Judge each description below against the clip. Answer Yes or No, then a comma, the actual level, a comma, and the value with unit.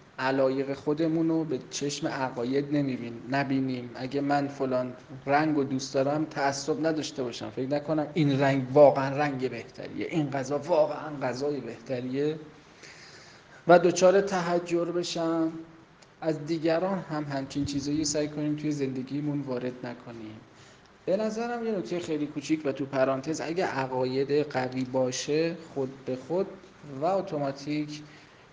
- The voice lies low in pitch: No, medium, 145 Hz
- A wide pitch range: No, average, 3.0 semitones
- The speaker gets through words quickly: No, average, 135 wpm